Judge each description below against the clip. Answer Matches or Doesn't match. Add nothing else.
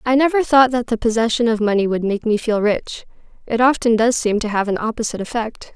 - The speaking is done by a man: Doesn't match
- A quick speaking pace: Matches